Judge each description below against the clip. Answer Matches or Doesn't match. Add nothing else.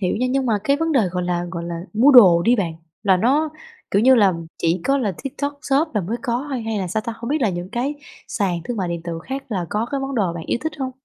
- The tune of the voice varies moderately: Doesn't match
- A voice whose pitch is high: Matches